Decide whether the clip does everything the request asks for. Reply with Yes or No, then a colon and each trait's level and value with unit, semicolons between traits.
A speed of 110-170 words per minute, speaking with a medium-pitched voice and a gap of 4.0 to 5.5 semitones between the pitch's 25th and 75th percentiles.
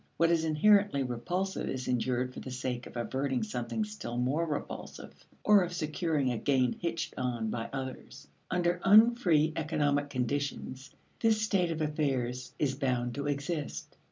Yes: average, 155 wpm; medium, 145 Hz; average, 5.0 semitones